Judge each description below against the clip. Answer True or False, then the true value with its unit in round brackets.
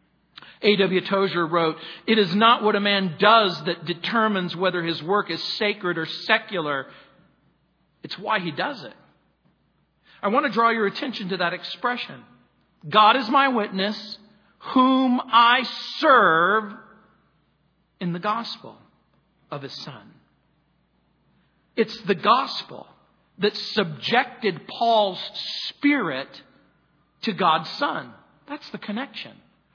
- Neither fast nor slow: False (120 wpm)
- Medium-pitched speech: False (210 Hz)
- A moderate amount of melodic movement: True (4.1 semitones)